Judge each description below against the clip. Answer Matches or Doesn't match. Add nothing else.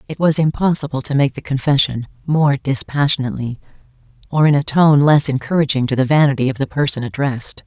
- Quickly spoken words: Doesn't match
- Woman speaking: Matches